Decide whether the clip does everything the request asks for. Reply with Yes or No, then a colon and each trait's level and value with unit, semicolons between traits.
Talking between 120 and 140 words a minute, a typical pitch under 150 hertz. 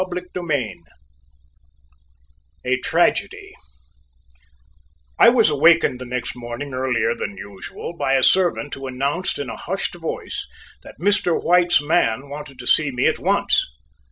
Yes: slow, 135 wpm; medium, 140 Hz